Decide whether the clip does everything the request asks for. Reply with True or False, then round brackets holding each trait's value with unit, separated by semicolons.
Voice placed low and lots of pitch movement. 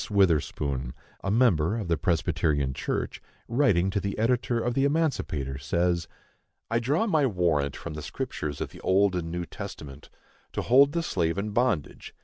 True (95 Hz; 7.5 semitones)